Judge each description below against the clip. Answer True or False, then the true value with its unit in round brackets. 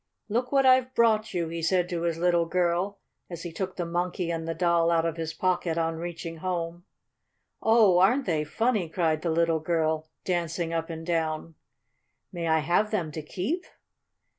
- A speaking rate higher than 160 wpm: True (185 wpm)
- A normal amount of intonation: False (2.1 semitones)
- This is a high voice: False (170 Hz)